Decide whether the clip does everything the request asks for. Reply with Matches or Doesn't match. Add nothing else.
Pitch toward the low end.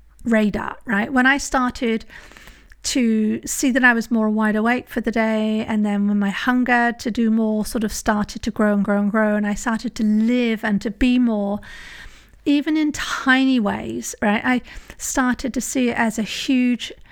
Doesn't match